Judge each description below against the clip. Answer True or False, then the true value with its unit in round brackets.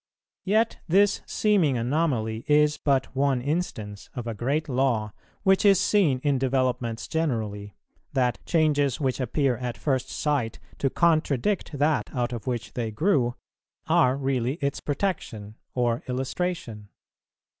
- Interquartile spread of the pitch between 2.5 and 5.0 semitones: True (4.4 semitones)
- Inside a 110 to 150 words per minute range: True (135 wpm)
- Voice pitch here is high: False (135 Hz)